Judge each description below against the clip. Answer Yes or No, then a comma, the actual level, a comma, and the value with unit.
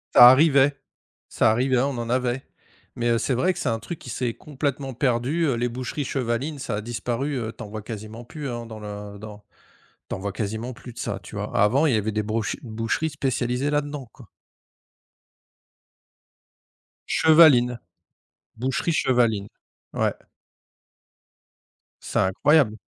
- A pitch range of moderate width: Yes, average, 3.7 semitones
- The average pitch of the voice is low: Yes, low, 120 Hz